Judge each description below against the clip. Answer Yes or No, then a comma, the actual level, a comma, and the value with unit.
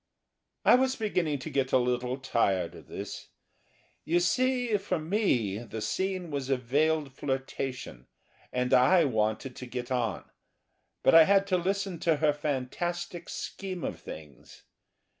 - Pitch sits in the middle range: Yes, medium, 145 Hz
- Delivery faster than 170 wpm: No, average, 145 wpm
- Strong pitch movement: Yes, wide, 6.3 semitones